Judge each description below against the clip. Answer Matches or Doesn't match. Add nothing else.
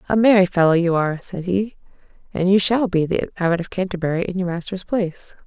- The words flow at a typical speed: Doesn't match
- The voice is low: Doesn't match